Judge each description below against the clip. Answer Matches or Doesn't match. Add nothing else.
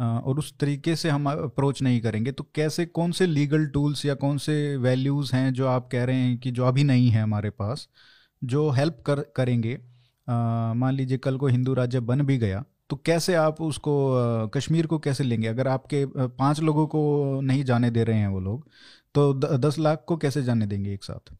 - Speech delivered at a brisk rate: Matches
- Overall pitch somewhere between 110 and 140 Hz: Matches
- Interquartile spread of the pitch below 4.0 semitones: Matches